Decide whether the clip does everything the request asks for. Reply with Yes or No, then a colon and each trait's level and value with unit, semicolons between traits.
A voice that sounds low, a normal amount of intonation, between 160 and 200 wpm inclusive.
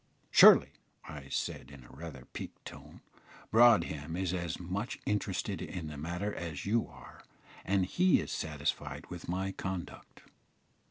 No: very low, 85 Hz; average, 4.4 semitones; average, 145 wpm